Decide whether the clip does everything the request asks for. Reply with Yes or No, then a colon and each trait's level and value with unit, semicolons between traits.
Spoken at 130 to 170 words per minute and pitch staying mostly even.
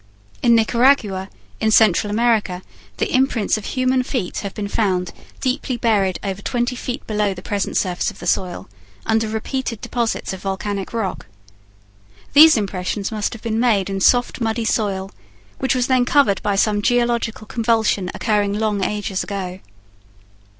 No: average, 155 wpm; average, 3.4 semitones